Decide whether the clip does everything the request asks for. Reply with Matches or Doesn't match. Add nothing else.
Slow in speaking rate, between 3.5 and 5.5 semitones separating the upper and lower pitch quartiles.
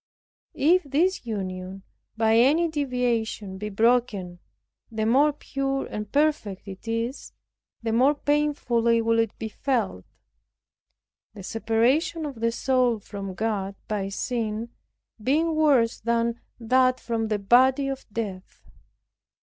Matches